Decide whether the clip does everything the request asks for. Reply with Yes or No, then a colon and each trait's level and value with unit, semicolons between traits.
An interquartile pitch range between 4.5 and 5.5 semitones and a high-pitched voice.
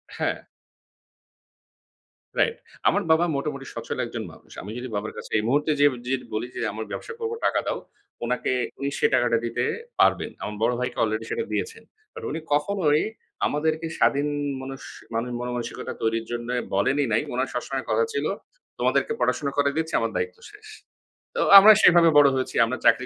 No: average, 4.9 semitones; medium, 140 Hz